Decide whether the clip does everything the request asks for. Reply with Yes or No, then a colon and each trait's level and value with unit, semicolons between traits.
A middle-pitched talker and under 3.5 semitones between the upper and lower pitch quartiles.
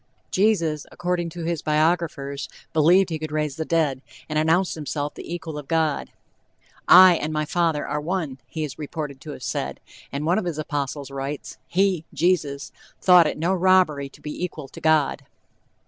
Yes: medium, 155 Hz; average, 2.8 semitones